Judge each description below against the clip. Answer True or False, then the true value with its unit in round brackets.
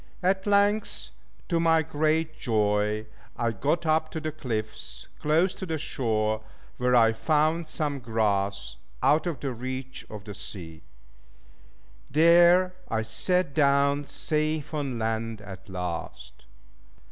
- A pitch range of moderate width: False (6.4 semitones)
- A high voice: False (140 Hz)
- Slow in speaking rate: True (130 wpm)